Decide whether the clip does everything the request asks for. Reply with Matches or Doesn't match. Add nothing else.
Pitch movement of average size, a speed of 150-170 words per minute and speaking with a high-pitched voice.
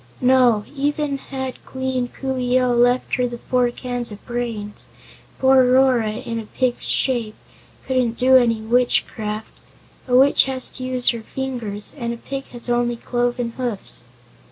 Doesn't match